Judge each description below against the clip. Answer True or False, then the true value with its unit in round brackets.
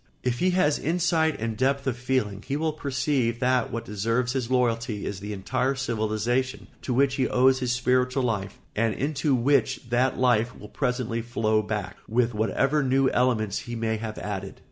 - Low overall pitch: True (125 Hz)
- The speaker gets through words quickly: False (180 wpm)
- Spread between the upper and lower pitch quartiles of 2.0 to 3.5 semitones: True (2.9 semitones)